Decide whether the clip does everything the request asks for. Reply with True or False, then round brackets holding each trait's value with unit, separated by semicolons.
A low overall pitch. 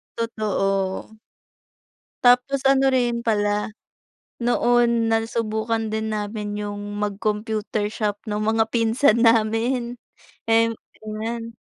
False (220 Hz)